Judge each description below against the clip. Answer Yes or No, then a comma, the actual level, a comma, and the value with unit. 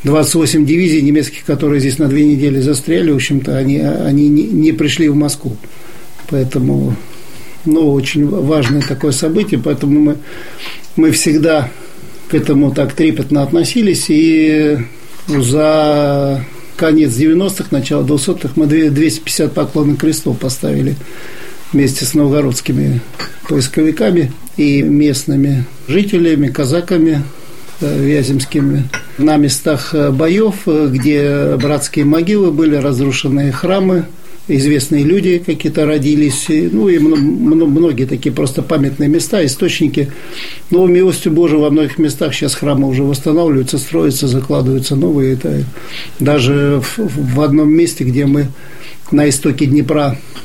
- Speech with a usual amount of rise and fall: No, narrow, 2.3 semitones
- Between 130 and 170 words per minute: No, average, 115 wpm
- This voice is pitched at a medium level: Yes, medium, 150 Hz